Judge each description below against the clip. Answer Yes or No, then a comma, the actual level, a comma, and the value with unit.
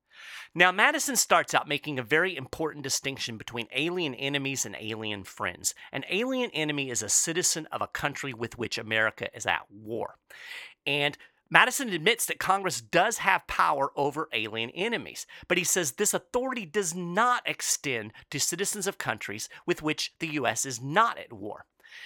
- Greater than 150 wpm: Yes, average, 165 wpm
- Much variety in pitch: Yes, wide, 7.5 semitones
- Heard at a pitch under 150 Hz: No, medium, 155 Hz